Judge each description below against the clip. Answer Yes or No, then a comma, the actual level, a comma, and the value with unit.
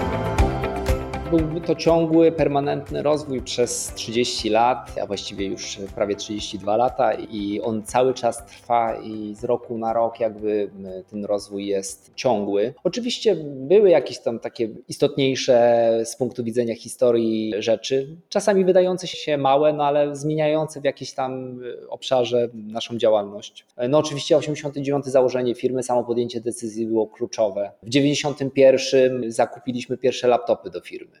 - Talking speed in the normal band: Yes, average, 135 wpm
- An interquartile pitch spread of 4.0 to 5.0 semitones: Yes, average, 4.5 semitones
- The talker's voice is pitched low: Yes, low, 120 Hz